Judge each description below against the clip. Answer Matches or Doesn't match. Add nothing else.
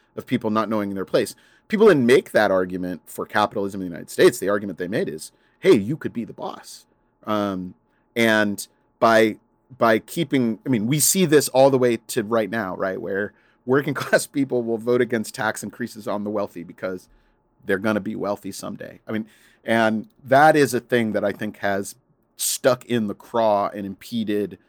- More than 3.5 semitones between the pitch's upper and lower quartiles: Doesn't match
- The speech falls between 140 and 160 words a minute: Doesn't match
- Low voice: Matches